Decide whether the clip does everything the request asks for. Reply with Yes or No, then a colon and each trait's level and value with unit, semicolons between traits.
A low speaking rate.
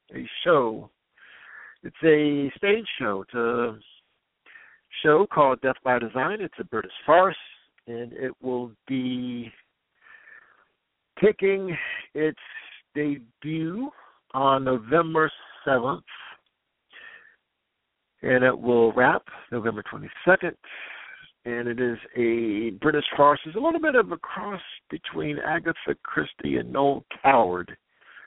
Yes: slow, 110 wpm